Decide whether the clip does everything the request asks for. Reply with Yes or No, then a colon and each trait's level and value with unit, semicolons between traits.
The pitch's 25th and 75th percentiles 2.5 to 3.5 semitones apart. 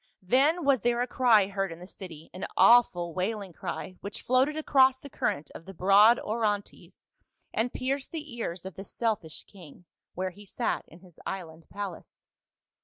No: average, 5.2 semitones